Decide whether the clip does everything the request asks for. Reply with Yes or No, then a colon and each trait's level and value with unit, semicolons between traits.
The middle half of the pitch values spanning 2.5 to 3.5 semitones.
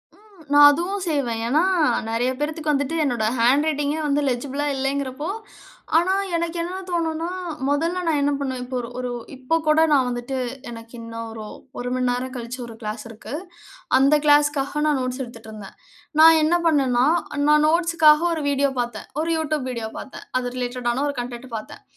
No: average, 3.9 semitones